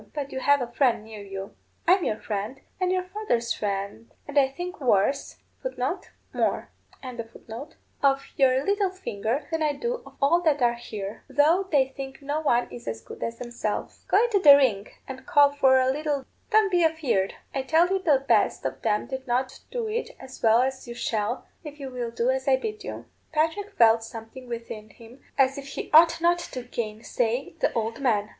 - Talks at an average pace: Yes, average, 190 wpm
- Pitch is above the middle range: Yes, very high, 265 Hz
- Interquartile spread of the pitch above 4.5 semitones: Yes, average, 5.0 semitones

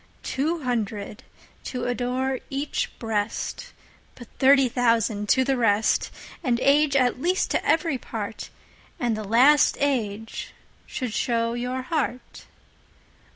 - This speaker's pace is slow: Yes, slow, 110 wpm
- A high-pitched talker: Yes, very high, 250 Hz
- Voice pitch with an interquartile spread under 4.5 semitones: Yes, average, 3.3 semitones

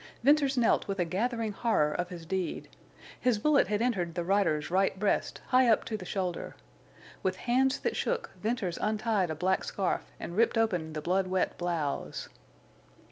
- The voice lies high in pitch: Yes, high, 195 Hz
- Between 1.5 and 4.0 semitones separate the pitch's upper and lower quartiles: No, average, 4.7 semitones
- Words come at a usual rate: Yes, average, 175 wpm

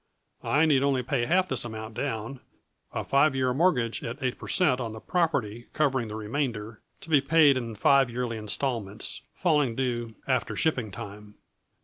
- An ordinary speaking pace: Yes, average, 170 wpm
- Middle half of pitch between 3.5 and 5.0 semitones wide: Yes, average, 3.8 semitones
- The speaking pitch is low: Yes, low, 125 Hz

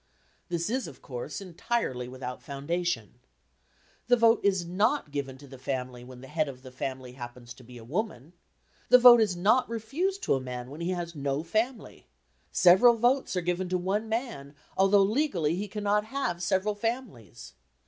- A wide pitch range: Yes, wide, 8.6 semitones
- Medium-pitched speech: Yes, medium, 175 Hz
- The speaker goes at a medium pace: Yes, average, 180 wpm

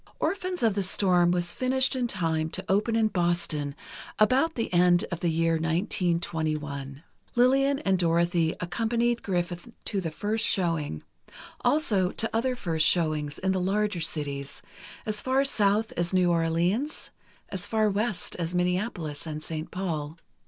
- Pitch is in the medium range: Yes, medium, 180 Hz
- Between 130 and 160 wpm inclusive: Yes, average, 145 wpm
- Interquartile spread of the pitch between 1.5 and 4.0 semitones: No, average, 4.8 semitones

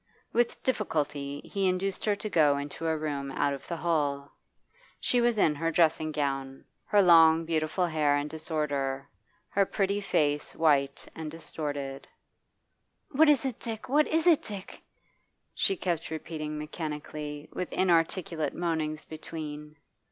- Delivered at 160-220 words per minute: No, average, 145 wpm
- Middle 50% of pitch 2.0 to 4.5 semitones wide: Yes, average, 4.0 semitones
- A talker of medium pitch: Yes, medium, 160 Hz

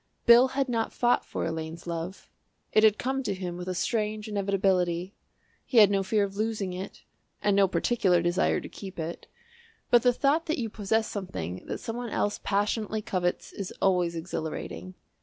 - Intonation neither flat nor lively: Yes, average, 3.7 semitones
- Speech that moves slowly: No, average, 180 wpm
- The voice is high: Yes, high, 200 Hz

